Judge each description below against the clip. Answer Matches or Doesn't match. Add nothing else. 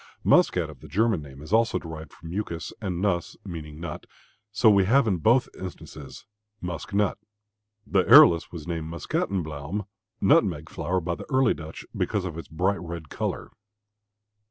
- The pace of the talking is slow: Doesn't match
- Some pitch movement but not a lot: Matches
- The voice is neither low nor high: Doesn't match